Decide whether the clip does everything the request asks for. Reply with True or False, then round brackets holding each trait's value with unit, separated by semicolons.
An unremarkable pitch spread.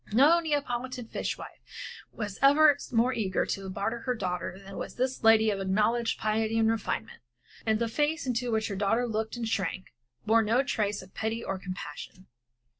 True (3.5 semitones)